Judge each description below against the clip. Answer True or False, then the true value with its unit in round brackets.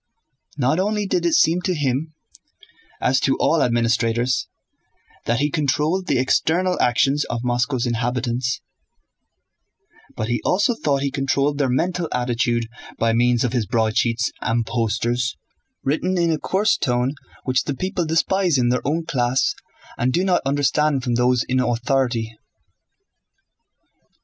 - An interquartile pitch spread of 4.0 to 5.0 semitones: True (4.4 semitones)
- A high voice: False (130 Hz)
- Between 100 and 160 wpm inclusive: True (140 wpm)